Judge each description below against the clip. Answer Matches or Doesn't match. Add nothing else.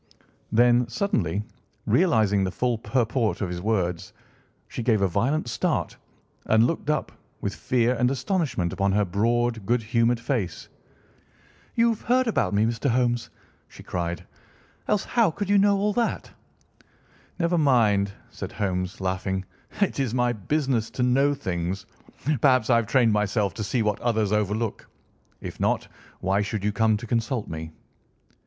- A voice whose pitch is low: Matches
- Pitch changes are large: Doesn't match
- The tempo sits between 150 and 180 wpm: Matches